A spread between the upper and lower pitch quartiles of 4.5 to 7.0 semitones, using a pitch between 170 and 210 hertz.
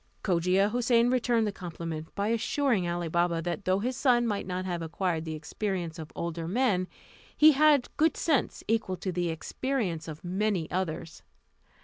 Yes: wide, 5.5 semitones; medium, 185 Hz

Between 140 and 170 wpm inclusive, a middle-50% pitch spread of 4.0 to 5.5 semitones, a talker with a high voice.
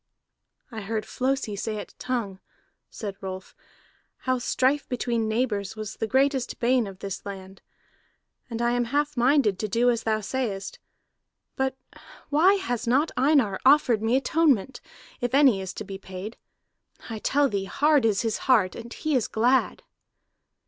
Yes: average, 155 wpm; average, 4.3 semitones; high, 235 Hz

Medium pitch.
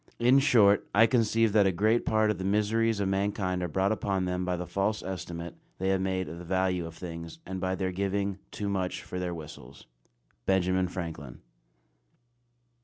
No: very low, 95 Hz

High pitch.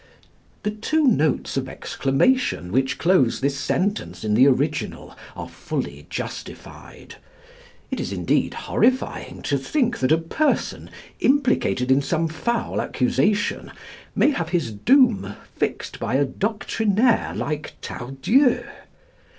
No: medium, 165 Hz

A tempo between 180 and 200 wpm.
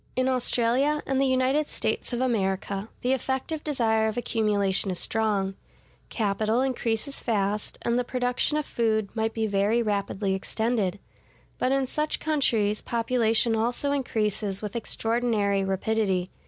No: average, 140 wpm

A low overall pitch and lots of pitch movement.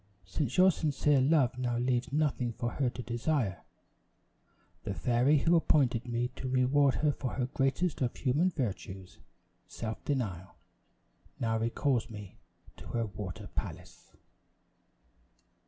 No: low, 125 Hz; average, 3.6 semitones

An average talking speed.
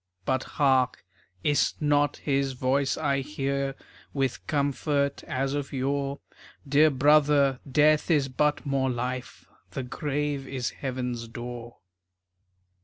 No: slow, 120 wpm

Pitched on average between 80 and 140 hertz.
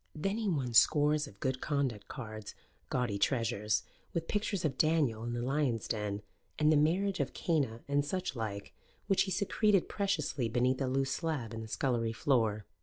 Yes: low, 135 Hz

